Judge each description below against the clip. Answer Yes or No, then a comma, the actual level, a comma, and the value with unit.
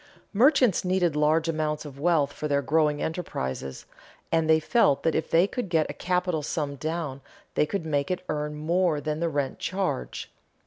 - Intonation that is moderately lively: Yes, average, 3.0 semitones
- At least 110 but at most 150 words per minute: No, average, 180 wpm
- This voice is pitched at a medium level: Yes, medium, 155 Hz